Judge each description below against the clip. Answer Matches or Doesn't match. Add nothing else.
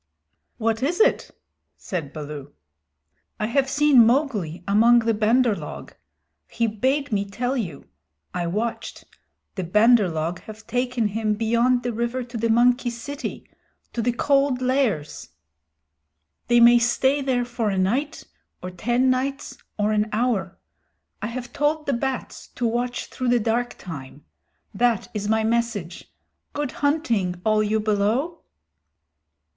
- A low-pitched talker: Doesn't match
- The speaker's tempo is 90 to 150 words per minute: Matches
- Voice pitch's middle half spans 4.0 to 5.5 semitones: Doesn't match